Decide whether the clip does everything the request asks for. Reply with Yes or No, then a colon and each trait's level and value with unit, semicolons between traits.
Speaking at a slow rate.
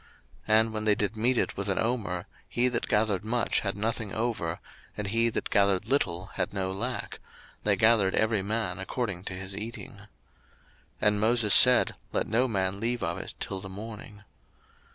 No: average, 185 wpm